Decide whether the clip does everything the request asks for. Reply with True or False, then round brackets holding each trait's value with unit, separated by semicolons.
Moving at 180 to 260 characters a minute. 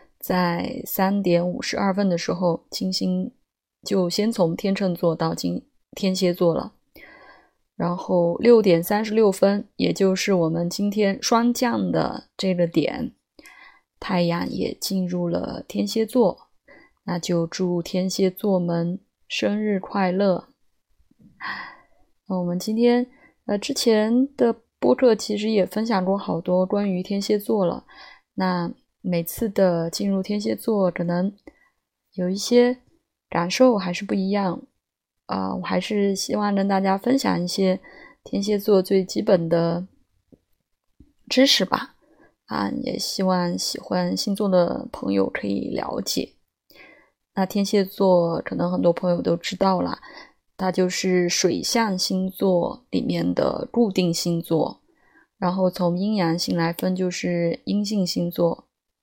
True (195 characters per minute)